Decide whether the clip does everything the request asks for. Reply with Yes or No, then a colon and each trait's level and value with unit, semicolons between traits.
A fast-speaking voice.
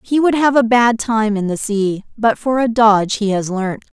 Yes: fast, 240 wpm